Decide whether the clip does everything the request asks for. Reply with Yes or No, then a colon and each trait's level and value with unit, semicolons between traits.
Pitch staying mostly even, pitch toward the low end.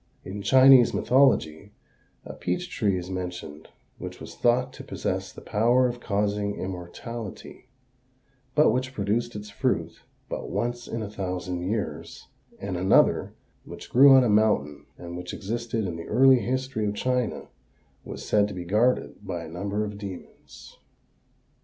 No: average, 4.7 semitones; low, 105 Hz